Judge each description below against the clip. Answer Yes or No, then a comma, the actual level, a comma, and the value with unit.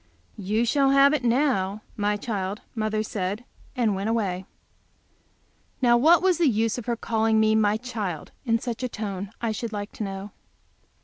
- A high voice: Yes, high, 220 Hz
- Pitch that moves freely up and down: No, average, 3.0 semitones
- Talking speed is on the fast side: No, average, 175 wpm